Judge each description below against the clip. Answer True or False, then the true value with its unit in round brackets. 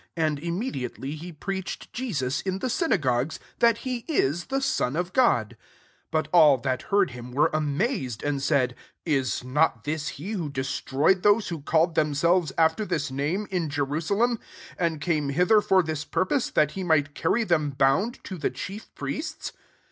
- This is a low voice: False (160 Hz)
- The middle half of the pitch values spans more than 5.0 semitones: True (5.4 semitones)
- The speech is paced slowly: False (180 wpm)